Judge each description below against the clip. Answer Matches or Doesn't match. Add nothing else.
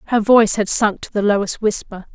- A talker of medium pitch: Doesn't match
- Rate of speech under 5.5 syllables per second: Doesn't match